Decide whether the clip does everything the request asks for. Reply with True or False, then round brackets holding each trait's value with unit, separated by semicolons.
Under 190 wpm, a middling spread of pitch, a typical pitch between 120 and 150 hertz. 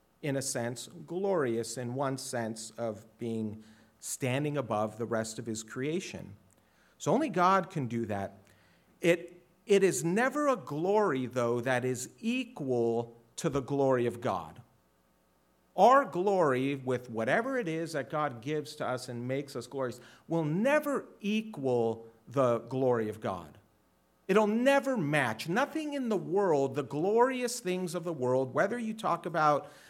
False (155 wpm; 7.4 semitones; 135 Hz)